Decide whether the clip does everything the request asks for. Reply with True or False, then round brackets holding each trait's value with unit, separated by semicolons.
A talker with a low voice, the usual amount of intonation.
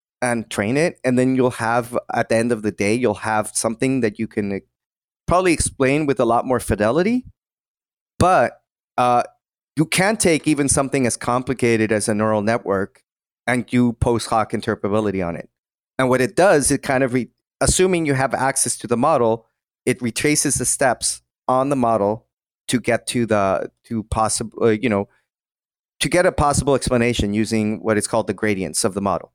True (120 Hz; 3.1 semitones)